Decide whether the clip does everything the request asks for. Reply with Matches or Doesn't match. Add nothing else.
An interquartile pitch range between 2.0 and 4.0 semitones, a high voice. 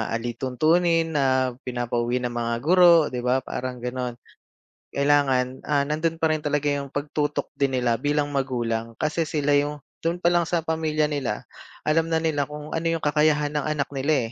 Doesn't match